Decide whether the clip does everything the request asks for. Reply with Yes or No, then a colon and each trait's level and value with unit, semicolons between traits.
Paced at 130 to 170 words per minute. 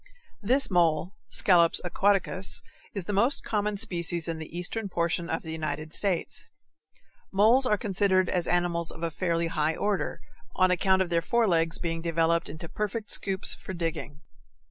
Yes: average, 160 wpm